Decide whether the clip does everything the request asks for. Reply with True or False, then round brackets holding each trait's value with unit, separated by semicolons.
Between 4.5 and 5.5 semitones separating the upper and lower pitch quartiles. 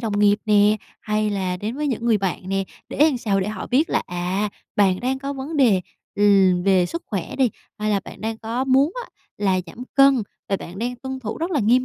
True (4.8 semitones)